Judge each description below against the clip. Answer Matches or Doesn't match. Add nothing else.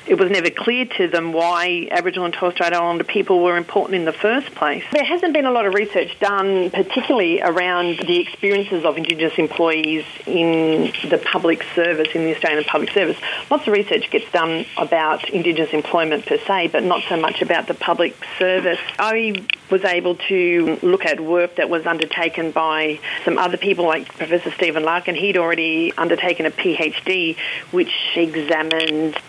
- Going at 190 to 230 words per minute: Doesn't match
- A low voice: Doesn't match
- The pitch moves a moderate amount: Matches